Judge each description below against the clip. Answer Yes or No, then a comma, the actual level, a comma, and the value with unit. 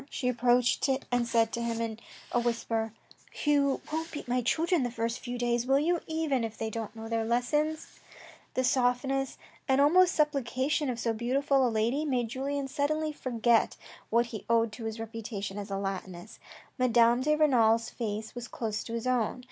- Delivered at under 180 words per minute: No, average, 190 wpm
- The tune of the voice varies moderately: Yes, average, 3.4 semitones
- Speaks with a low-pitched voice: No, high, 245 Hz